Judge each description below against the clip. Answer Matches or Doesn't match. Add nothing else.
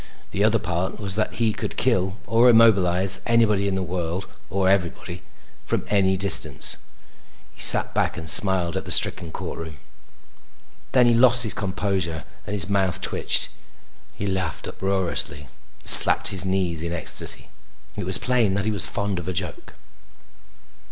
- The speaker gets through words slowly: Doesn't match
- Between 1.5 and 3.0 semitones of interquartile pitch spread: Matches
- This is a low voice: Matches